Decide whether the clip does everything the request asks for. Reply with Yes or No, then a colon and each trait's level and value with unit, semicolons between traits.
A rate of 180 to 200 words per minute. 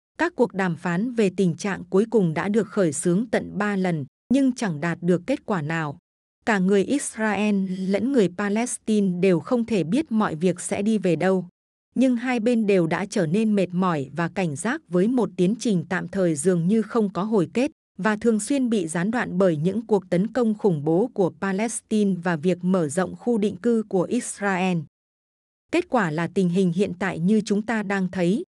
No: average, 210 wpm